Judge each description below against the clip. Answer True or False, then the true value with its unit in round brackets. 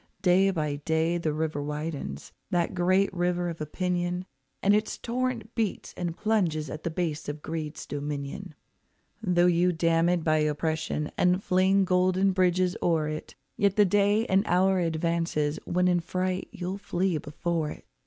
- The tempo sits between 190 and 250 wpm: False (160 wpm)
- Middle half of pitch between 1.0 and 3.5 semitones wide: True (2.9 semitones)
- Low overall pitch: False (175 Hz)